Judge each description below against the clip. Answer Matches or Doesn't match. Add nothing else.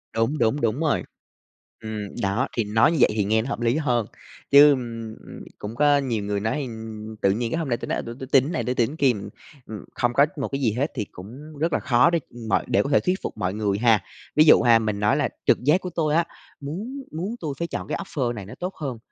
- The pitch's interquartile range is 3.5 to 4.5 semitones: Doesn't match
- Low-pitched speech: Matches